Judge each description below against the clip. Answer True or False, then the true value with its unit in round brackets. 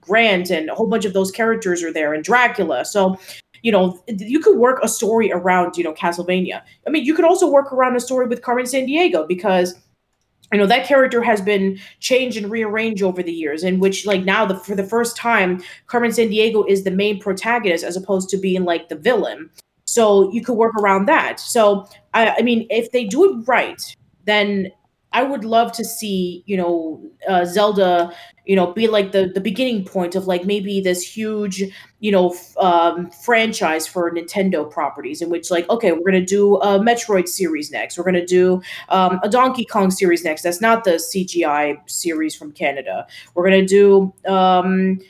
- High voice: True (195 Hz)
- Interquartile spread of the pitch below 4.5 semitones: True (3.9 semitones)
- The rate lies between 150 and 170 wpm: False (200 wpm)